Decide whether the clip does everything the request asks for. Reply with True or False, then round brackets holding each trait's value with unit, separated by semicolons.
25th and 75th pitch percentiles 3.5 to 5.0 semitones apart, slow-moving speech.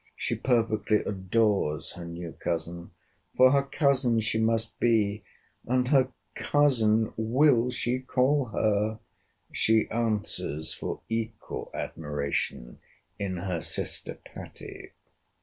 True (4.3 semitones; 105 wpm)